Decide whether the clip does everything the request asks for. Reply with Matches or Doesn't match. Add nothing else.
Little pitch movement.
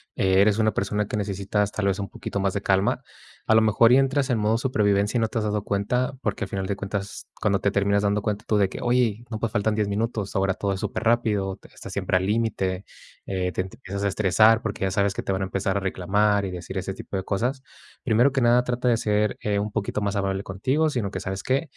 Matches